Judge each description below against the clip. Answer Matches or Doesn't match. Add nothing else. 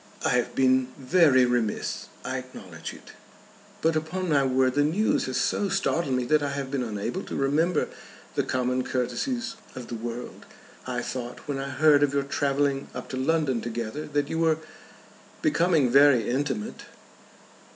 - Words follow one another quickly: Doesn't match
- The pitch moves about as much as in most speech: Matches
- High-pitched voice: Doesn't match